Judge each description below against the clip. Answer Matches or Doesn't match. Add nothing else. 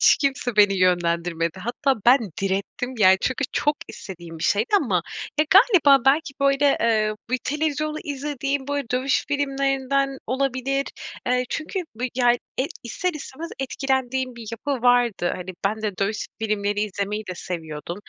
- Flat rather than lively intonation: Doesn't match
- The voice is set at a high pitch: Matches